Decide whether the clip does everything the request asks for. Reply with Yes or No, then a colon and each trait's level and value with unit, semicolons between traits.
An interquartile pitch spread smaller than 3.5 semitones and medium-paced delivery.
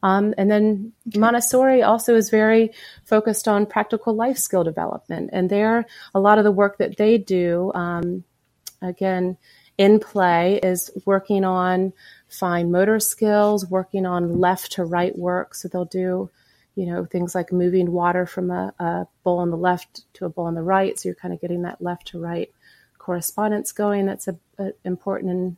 Yes: average, 2.7 semitones; average, 180 wpm